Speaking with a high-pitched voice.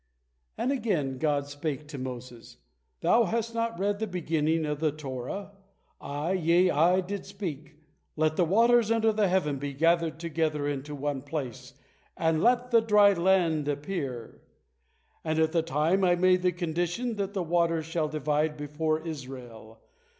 No: medium, 160 Hz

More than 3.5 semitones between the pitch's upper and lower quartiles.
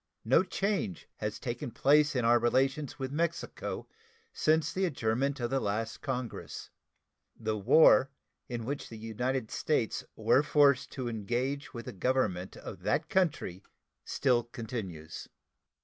Yes: average, 4.1 semitones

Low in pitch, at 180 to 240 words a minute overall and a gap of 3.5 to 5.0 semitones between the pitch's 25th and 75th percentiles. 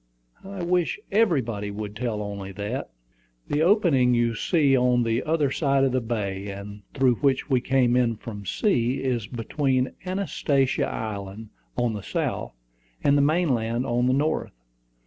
No: low, 125 Hz; average, 160 wpm; average, 4.3 semitones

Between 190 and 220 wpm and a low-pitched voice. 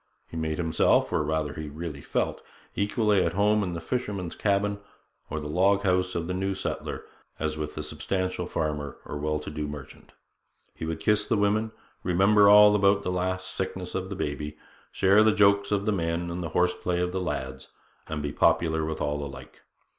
Yes: average, 200 wpm; very low, 90 Hz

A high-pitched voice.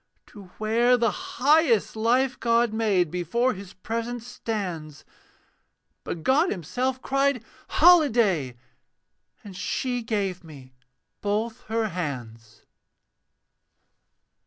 Yes: high, 220 Hz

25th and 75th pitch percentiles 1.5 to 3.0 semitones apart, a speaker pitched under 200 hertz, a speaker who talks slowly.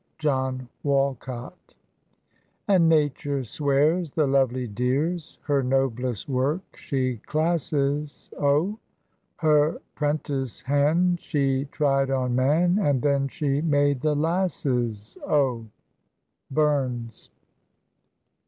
Yes: average, 2.7 semitones; medium, 140 Hz; slow, 95 wpm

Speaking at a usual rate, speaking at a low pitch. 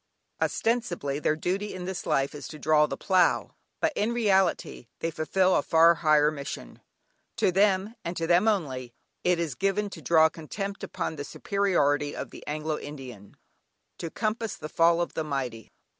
No: average, 175 wpm; medium, 165 Hz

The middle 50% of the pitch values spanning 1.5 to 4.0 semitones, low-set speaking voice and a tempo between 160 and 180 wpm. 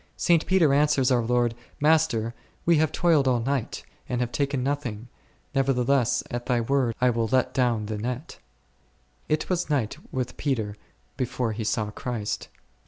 Yes: average, 3.4 semitones; low, 125 Hz; average, 165 wpm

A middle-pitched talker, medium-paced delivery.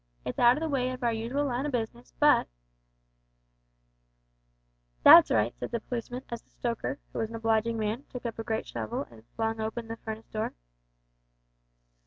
No: high, 225 Hz; average, 185 wpm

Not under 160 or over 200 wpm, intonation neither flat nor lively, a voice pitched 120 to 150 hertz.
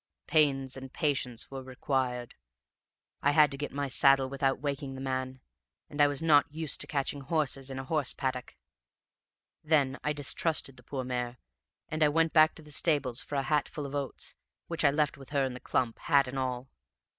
No: average, 195 wpm; narrow, 2.1 semitones; medium, 140 Hz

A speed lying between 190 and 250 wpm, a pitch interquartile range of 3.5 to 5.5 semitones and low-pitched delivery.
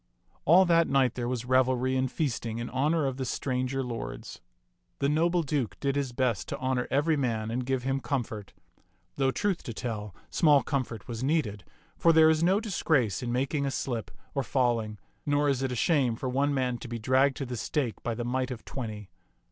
No: fast, 205 wpm; average, 2.9 semitones; low, 130 Hz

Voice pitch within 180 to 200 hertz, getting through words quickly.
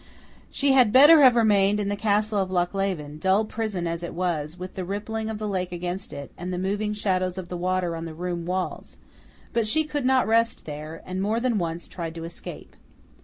Yes: high, 190 Hz; fast, 215 wpm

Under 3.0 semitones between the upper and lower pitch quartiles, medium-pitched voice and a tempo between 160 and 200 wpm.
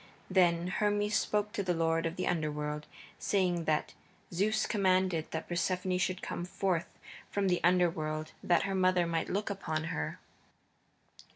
No: narrow, 2.6 semitones; medium, 180 Hz; average, 150 wpm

